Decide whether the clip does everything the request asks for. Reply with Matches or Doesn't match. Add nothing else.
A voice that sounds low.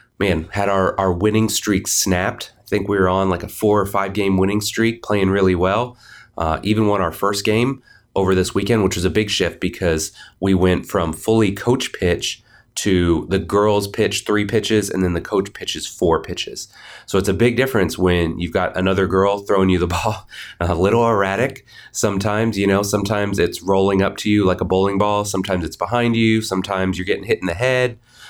Matches